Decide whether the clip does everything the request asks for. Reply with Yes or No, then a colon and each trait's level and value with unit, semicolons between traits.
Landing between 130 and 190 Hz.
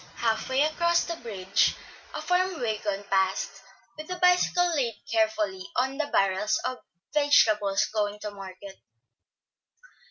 No: high, 225 Hz